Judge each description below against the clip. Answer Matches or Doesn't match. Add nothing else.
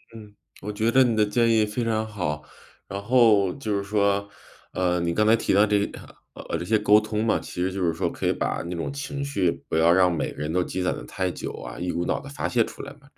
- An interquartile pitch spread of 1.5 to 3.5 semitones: Doesn't match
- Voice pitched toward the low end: Matches